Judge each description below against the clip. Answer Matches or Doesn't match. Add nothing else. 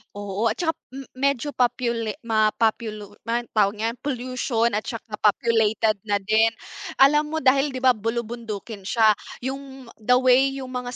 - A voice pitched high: Matches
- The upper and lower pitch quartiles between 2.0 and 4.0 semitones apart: Matches